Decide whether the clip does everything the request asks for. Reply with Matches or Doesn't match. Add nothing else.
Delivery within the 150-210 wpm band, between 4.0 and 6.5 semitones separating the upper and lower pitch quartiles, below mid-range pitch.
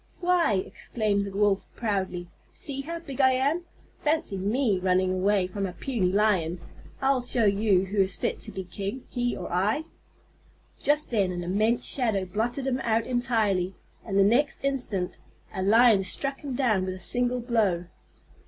Doesn't match